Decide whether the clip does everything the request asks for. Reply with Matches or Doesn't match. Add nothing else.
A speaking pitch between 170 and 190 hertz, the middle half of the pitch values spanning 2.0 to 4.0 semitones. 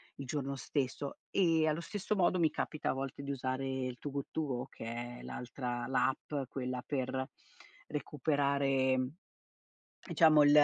Doesn't match